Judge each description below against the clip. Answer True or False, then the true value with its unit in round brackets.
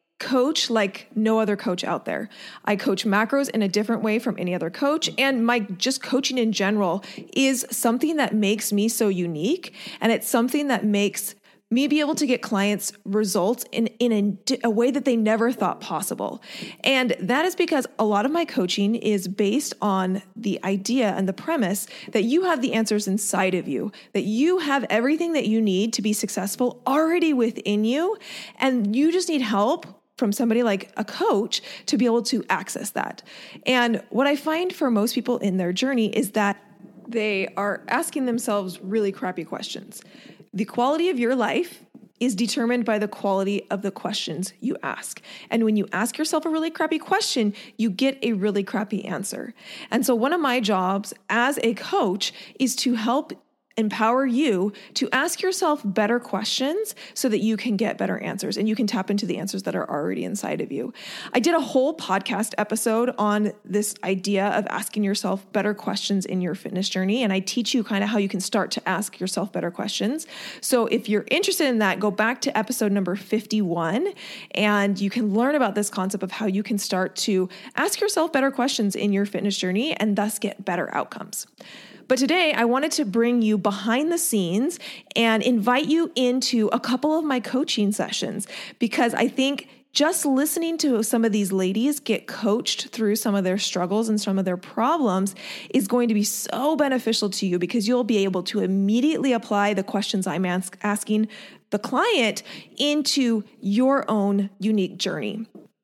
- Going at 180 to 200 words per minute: True (190 wpm)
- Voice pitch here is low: False (220 Hz)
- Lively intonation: False (4.3 semitones)